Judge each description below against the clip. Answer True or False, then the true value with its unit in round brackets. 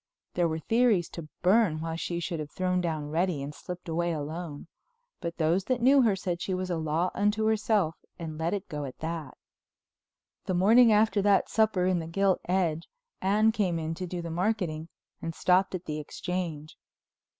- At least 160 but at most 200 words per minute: True (190 wpm)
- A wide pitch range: False (3.4 semitones)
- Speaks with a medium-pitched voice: True (175 Hz)